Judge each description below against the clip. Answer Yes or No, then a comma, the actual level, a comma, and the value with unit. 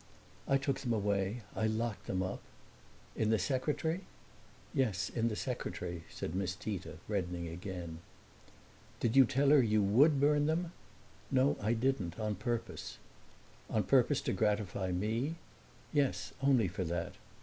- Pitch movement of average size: No, wide, 6.1 semitones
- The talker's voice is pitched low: Yes, low, 110 Hz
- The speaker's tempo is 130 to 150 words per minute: Yes, average, 145 wpm